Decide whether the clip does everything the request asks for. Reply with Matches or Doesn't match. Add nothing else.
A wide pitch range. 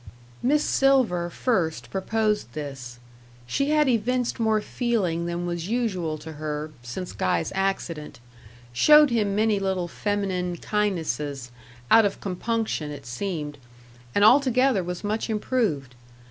Matches